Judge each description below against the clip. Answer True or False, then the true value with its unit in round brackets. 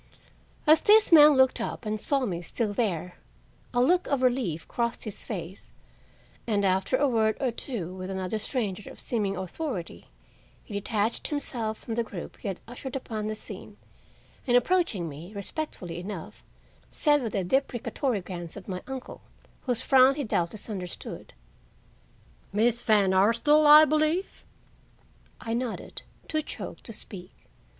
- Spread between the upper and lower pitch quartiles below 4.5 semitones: False (5.5 semitones)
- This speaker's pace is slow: False (150 wpm)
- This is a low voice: False (225 Hz)